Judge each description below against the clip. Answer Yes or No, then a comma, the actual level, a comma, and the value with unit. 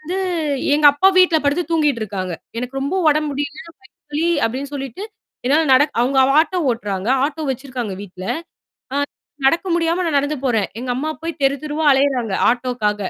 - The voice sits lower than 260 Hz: No, very high, 280 Hz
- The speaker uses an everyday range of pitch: Yes, average, 4.0 semitones